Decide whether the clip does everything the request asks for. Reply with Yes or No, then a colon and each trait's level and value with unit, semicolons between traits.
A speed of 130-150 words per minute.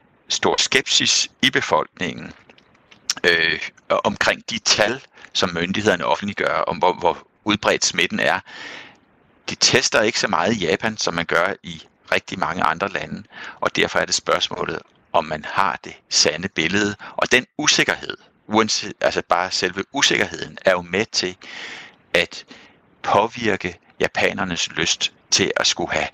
Yes: slow, 145 wpm